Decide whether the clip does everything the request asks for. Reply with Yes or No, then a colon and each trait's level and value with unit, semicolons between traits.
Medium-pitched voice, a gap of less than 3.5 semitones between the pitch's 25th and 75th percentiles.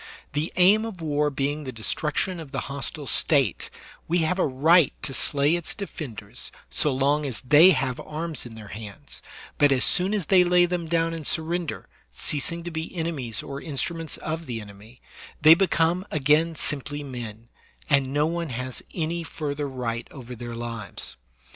No: medium, 150 Hz; average, 4.3 semitones